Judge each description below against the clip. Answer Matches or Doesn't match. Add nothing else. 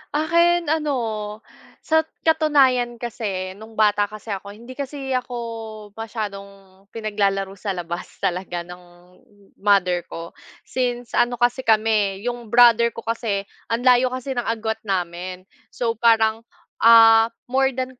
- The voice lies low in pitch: Doesn't match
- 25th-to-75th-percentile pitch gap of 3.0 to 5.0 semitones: Matches